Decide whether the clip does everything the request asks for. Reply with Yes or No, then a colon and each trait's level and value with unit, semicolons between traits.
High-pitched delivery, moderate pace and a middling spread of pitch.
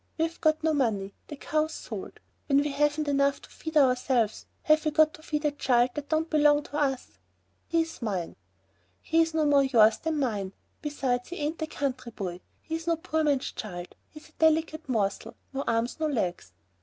Yes: very high, 290 Hz; average, 190 wpm; average, 4.2 semitones